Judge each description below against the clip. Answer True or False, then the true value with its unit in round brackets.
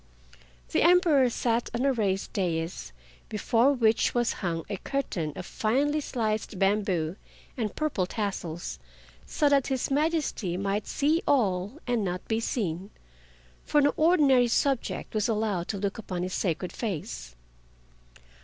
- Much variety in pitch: True (6.4 semitones)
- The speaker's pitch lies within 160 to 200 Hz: False (220 Hz)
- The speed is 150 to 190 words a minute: False (140 wpm)